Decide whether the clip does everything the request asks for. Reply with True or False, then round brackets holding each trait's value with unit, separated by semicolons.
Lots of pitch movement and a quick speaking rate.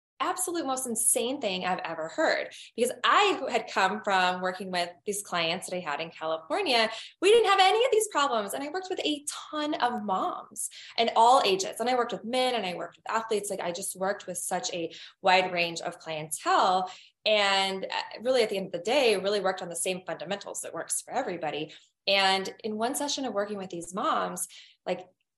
True (5.8 semitones; 210 wpm)